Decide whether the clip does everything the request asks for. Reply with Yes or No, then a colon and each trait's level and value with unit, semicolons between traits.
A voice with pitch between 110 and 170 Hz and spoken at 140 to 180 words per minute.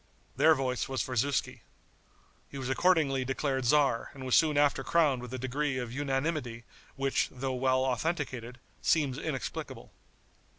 Yes: low, 135 Hz; average, 145 wpm